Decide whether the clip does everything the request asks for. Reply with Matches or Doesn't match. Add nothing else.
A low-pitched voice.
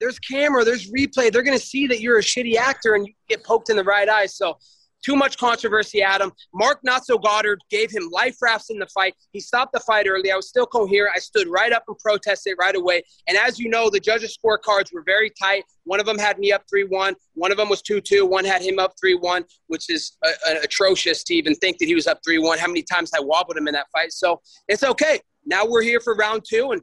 Doesn't match